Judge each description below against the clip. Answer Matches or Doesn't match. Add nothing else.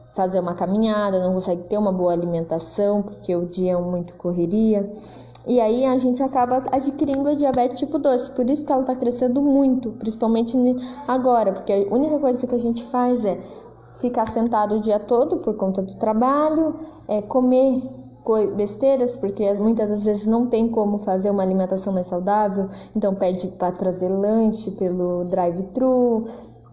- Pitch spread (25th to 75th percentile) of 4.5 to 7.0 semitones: Matches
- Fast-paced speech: Doesn't match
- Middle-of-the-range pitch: Doesn't match